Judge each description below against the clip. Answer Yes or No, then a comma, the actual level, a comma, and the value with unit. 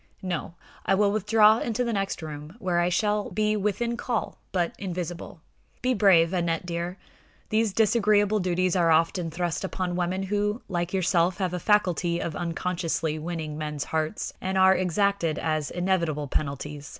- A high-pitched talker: No, medium, 180 Hz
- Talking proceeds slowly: No, average, 160 wpm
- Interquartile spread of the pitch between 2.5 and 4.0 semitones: Yes, average, 3.5 semitones